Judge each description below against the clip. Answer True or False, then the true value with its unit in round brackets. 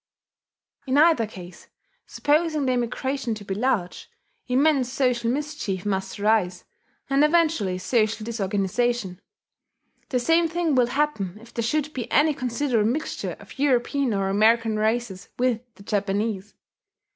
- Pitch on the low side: False (235 Hz)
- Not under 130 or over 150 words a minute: True (135 wpm)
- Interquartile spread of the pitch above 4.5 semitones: True (5.1 semitones)